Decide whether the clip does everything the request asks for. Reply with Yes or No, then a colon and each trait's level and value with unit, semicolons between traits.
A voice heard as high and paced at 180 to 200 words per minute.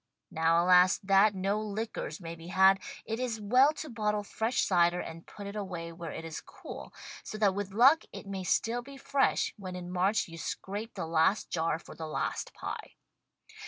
Yes: high, 195 Hz; average, 195 wpm